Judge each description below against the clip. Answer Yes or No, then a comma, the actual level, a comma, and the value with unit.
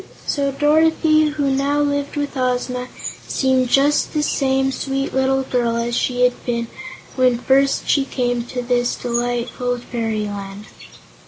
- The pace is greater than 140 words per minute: No, slow, 135 wpm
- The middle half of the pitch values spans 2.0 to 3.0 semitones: Yes, narrow, 2.4 semitones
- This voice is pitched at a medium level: No, very high, 255 Hz